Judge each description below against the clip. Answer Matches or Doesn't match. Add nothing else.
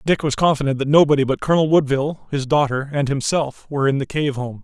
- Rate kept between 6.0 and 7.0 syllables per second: Matches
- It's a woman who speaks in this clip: Doesn't match